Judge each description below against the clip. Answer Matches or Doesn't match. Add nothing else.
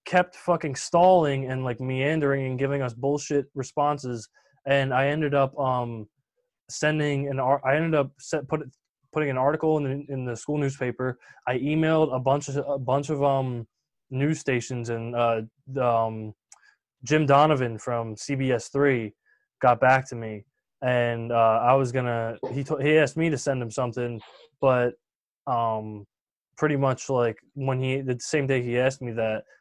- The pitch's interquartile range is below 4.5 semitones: Matches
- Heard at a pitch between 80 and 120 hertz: Doesn't match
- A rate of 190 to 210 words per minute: Doesn't match